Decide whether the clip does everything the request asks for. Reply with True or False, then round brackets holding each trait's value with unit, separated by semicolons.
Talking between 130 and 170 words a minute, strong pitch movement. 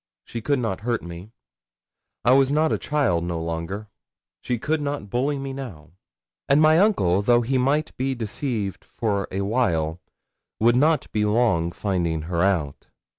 True (165 wpm; 7.1 semitones)